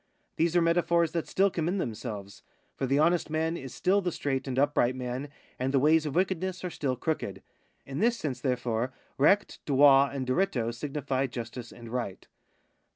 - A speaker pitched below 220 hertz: Yes, medium, 140 Hz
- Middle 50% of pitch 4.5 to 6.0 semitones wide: Yes, average, 4.8 semitones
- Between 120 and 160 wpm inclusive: No, average, 175 wpm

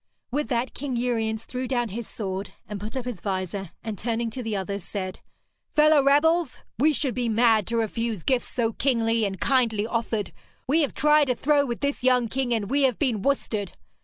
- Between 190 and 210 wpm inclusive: Yes, average, 200 wpm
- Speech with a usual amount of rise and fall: Yes, average, 3.7 semitones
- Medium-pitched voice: No, high, 235 Hz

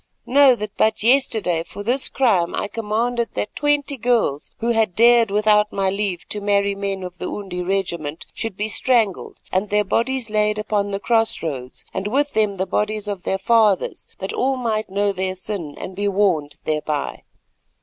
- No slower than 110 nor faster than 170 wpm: No, average, 180 wpm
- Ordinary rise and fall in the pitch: Yes, average, 3.1 semitones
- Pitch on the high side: Yes, high, 205 Hz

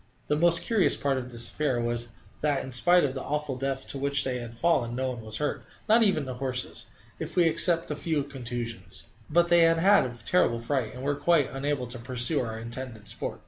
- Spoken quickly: Yes, fast, 225 wpm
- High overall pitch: No, low, 135 Hz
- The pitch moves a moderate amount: Yes, average, 4.1 semitones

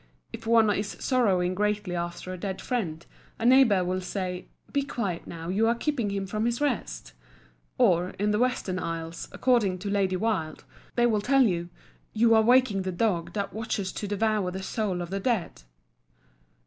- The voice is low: No, high, 200 Hz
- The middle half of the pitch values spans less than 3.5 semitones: No, average, 3.8 semitones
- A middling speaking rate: Yes, average, 180 wpm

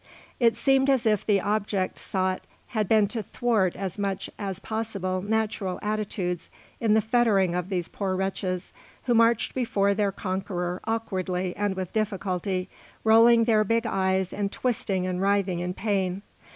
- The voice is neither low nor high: No, high, 200 Hz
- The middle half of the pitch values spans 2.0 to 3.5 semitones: Yes, average, 2.9 semitones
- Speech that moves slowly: No, average, 155 wpm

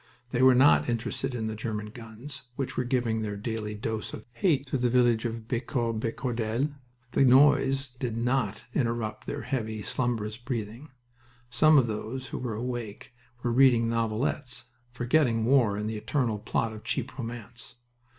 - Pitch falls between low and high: No, low, 120 Hz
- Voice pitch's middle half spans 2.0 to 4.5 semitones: Yes, average, 2.7 semitones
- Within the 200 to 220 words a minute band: No, average, 160 wpm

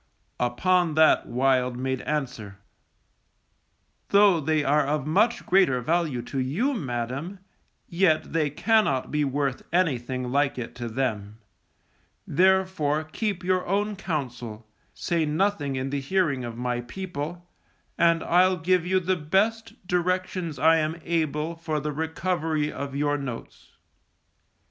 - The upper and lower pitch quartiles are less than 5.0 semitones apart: No, average, 5.3 semitones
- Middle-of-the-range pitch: Yes, medium, 155 Hz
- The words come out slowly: Yes, slow, 130 wpm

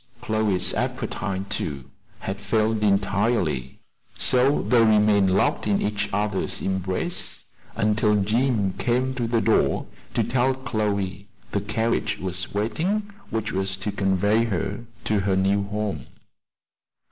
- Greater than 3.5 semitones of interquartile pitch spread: No, average, 2.9 semitones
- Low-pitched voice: Yes, low, 105 Hz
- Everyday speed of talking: No, slow, 125 wpm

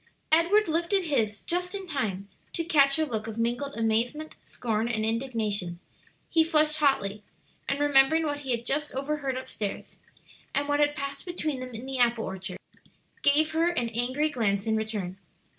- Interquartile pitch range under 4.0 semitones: No, wide, 5.4 semitones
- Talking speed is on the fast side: No, average, 175 wpm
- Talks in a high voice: Yes, very high, 270 Hz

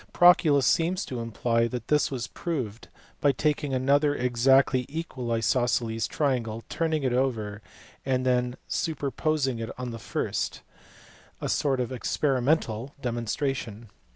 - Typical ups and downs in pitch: Yes, average, 3.5 semitones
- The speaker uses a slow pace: Yes, slow, 125 wpm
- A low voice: Yes, low, 130 Hz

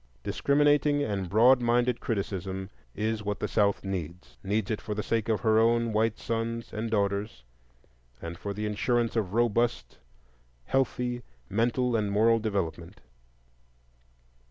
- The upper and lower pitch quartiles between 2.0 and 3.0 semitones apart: Yes, average, 2.7 semitones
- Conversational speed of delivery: No, slow, 130 wpm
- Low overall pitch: Yes, low, 110 Hz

